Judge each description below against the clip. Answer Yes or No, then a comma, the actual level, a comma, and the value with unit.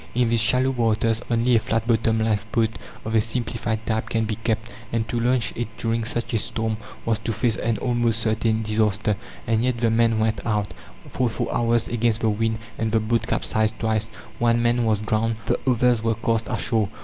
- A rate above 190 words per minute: Yes, average, 200 wpm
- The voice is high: No, low, 115 Hz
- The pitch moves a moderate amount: No, narrow, 1.1 semitones